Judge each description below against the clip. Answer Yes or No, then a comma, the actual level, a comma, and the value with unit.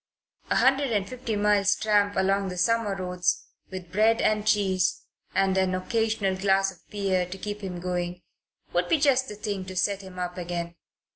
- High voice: Yes, high, 195 Hz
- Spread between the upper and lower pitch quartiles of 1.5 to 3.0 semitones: Yes, narrow, 2.5 semitones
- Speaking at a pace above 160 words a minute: Yes, average, 185 wpm